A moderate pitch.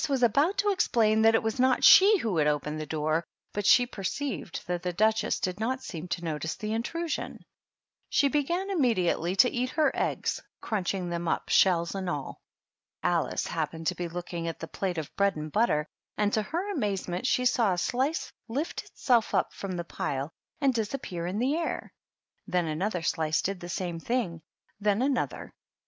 No: high, 200 Hz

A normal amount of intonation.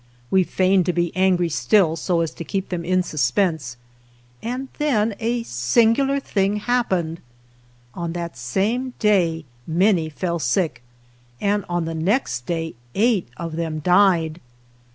Yes: average, 4.2 semitones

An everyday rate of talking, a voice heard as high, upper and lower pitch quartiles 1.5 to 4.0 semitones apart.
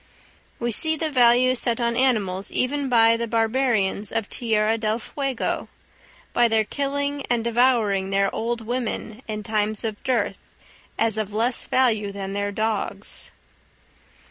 Yes: average, 145 wpm; high, 230 Hz; average, 2.9 semitones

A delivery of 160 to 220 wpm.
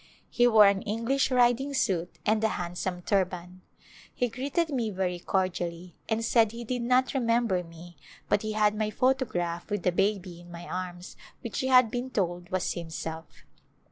Yes: average, 175 wpm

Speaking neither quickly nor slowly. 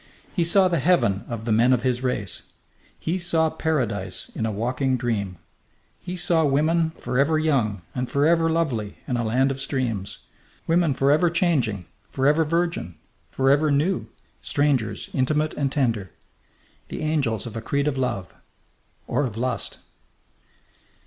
Yes: average, 145 wpm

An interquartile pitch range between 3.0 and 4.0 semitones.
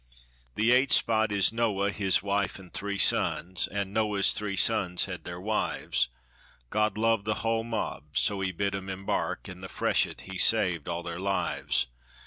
No: narrow, 2.5 semitones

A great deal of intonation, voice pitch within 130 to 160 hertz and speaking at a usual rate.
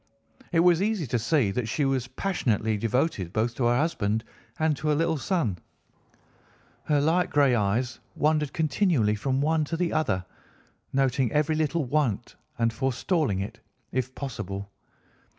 Yes: wide, 5.7 semitones; low, 135 Hz; average, 150 wpm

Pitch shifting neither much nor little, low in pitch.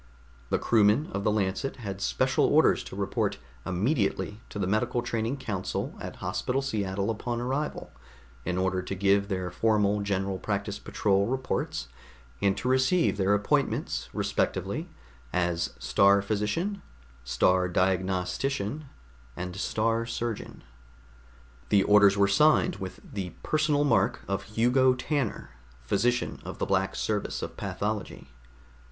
Yes: average, 4.1 semitones; low, 105 Hz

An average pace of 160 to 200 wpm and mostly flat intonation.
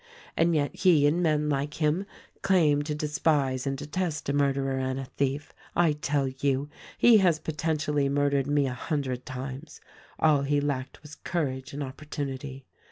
Yes: average, 165 wpm; narrow, 2.1 semitones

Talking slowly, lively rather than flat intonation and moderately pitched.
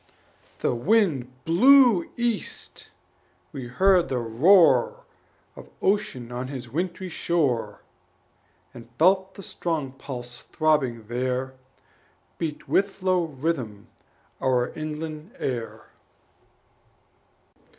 Yes: slow, 95 wpm; wide, 6.9 semitones; medium, 155 Hz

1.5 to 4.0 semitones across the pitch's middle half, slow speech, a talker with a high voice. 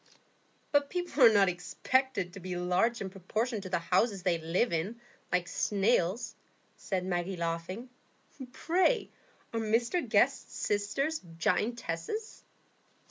No: average, 5.2 semitones; slow, 125 wpm; high, 200 Hz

